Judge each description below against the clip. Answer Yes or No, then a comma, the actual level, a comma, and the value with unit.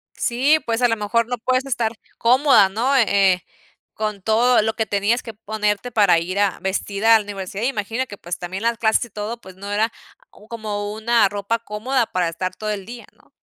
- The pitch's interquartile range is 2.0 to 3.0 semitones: Yes, average, 2.7 semitones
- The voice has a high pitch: Yes, high, 215 Hz